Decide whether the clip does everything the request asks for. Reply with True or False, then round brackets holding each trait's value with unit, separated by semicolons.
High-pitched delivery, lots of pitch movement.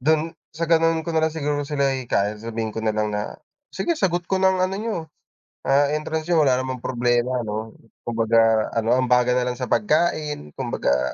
False (130 Hz; 5.8 semitones)